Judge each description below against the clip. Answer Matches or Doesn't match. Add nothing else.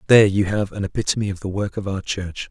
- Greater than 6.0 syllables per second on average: Matches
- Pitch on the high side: Doesn't match